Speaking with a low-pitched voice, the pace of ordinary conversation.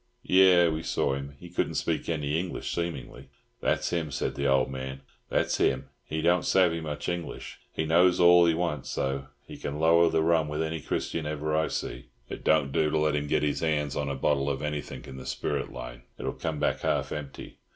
No: very low, 75 Hz; fast, 215 wpm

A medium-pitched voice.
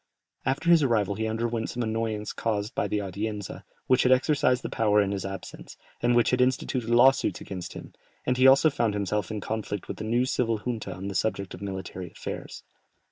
No: low, 110 Hz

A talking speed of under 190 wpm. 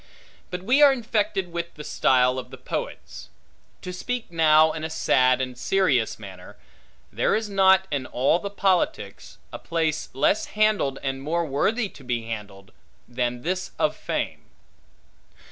Yes: average, 155 wpm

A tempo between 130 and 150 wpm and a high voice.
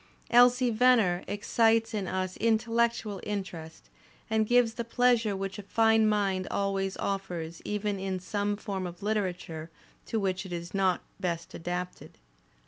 Yes: average, 140 wpm; high, 200 Hz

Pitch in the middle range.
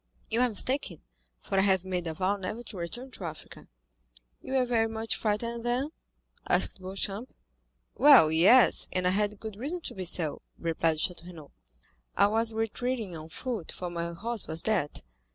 No: high, 205 Hz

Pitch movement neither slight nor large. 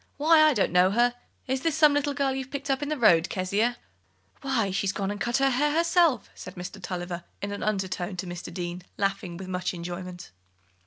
No: wide, 7.0 semitones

